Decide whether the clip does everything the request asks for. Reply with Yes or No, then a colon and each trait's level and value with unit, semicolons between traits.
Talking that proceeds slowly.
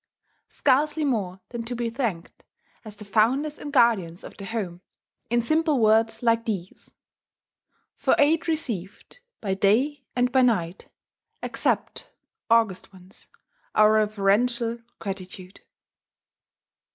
Yes: slow, 115 wpm